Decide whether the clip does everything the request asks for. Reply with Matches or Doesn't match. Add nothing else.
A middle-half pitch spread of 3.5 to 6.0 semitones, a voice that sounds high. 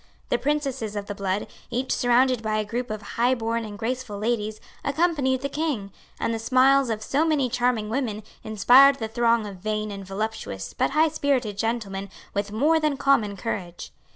Matches